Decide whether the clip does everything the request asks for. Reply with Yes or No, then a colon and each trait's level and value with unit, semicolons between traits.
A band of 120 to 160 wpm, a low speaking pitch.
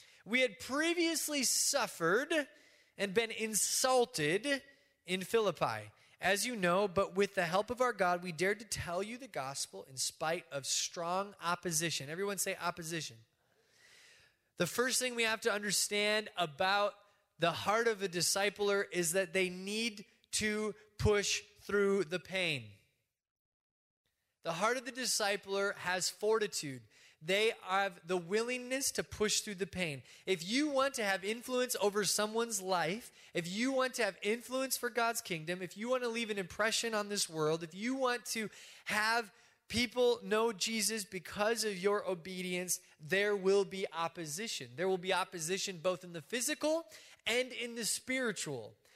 No: average, 155 wpm; high, 205 Hz